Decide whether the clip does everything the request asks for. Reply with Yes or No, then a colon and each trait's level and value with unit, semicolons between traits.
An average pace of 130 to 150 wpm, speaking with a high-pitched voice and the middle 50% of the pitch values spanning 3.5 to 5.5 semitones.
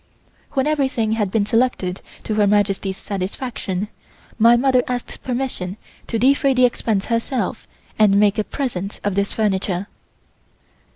Yes: slow, 135 wpm; high, 215 Hz; average, 3.9 semitones